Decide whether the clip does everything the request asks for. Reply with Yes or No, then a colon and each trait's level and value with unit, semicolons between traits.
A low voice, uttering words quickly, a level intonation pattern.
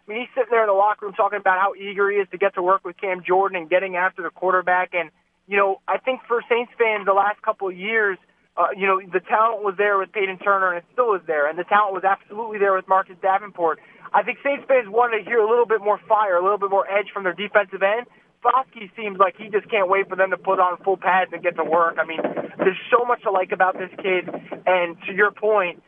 No: high, 195 Hz; fast, 275 wpm; narrow, 2.2 semitones